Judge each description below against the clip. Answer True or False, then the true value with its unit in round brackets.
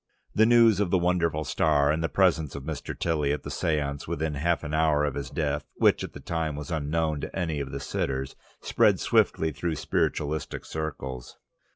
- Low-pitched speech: True (75 Hz)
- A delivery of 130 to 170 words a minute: False (195 wpm)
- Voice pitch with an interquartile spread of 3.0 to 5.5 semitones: False (2.4 semitones)